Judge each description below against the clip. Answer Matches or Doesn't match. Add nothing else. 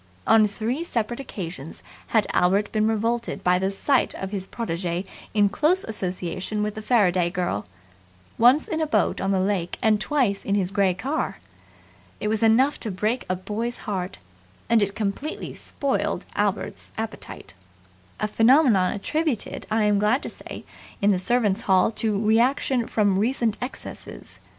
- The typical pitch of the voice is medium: Doesn't match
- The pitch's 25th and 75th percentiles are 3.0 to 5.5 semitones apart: Matches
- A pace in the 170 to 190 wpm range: Doesn't match